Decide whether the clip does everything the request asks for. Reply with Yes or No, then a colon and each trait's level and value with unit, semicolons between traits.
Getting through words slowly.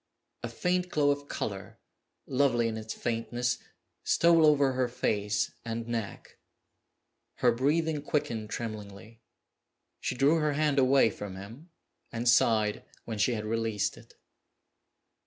Yes: slow, 130 wpm